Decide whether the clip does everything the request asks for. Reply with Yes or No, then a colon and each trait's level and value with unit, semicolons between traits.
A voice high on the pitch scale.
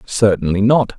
No: low, 105 Hz